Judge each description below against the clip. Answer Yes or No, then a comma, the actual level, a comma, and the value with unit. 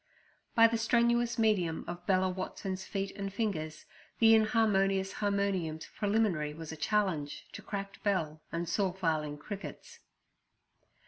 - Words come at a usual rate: No, slow, 130 wpm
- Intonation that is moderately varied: Yes, average, 4.4 semitones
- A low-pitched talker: No, high, 195 Hz